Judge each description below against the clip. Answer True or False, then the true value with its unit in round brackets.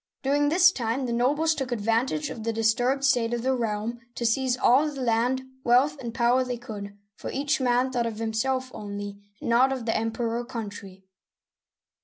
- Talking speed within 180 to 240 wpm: True (190 wpm)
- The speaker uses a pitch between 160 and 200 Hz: False (240 Hz)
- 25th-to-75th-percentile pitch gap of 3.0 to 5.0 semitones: False (2.6 semitones)